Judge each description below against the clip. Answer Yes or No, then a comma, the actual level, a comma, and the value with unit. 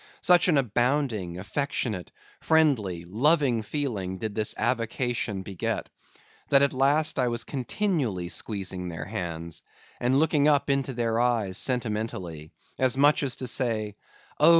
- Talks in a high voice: No, low, 120 Hz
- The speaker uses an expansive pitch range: Yes, wide, 5.9 semitones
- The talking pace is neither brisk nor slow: No, slow, 130 wpm